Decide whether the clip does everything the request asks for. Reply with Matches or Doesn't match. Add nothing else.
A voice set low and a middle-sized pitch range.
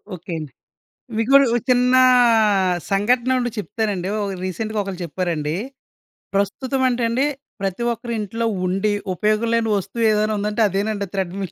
Doesn't match